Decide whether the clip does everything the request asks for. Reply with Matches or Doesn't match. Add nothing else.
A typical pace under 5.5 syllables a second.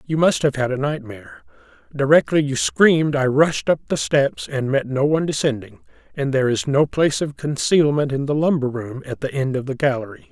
Doesn't match